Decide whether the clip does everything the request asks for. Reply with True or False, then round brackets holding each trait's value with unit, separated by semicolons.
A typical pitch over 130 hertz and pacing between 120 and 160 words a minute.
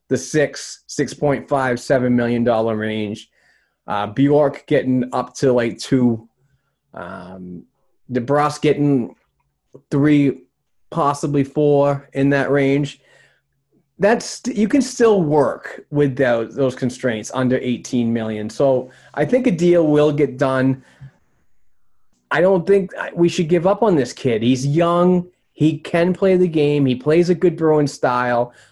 True (140 Hz; 140 wpm)